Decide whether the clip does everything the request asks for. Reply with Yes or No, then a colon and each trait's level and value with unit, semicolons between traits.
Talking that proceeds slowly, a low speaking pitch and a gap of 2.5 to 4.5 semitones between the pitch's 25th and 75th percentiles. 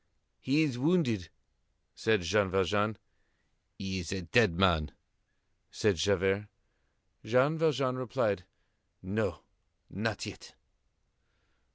No: slow, 95 wpm; low, 105 Hz; average, 5.0 semitones